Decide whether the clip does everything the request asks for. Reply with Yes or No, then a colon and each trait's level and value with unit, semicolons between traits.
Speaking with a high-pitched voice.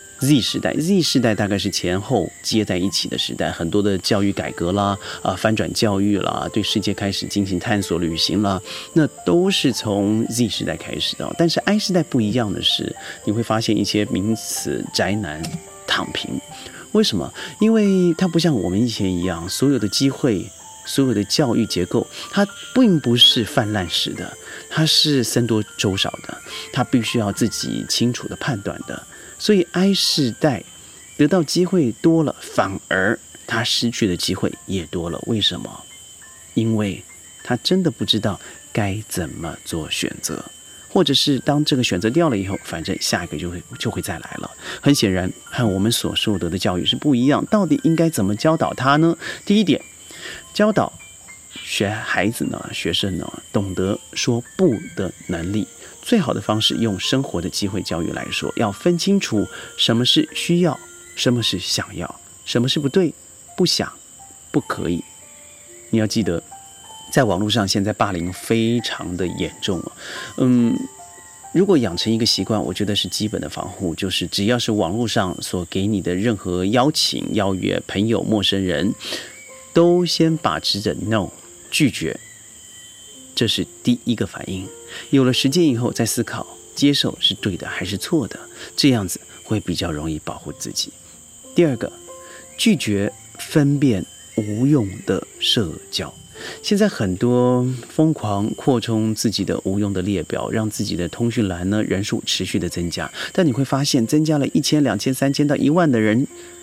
No: low, 115 Hz